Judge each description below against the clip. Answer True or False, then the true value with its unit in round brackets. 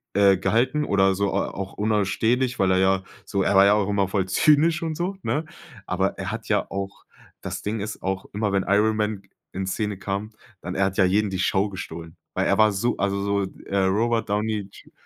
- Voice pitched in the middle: False (100 Hz)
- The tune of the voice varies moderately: False (2.0 semitones)